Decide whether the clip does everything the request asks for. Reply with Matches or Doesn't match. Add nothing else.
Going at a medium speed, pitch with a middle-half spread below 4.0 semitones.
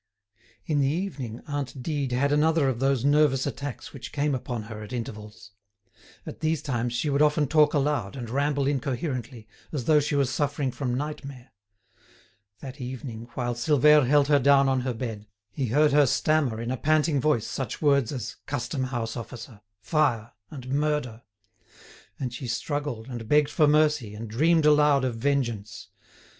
Matches